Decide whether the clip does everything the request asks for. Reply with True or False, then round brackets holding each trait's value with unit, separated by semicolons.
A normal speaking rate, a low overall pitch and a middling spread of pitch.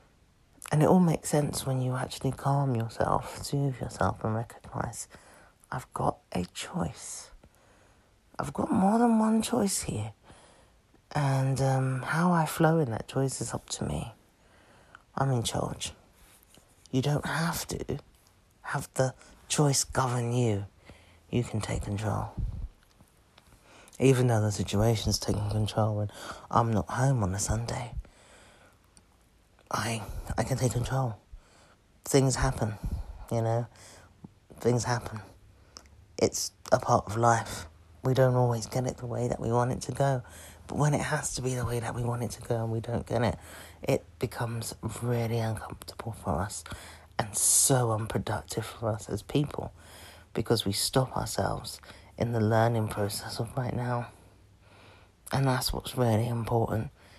True (150 wpm; 115 Hz; 4.4 semitones)